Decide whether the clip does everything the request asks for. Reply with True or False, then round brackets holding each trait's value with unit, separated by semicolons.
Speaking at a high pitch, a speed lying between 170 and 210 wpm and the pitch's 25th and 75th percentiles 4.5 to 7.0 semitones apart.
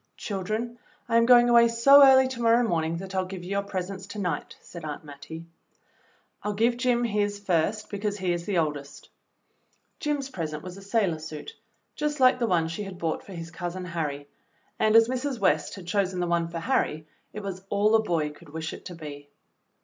True (195 Hz; 205 wpm; 5.4 semitones)